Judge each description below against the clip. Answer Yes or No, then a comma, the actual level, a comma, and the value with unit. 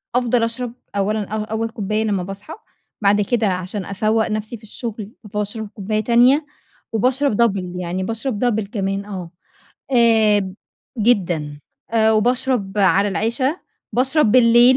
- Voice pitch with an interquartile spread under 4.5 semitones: Yes, average, 2.9 semitones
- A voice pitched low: No, high, 215 Hz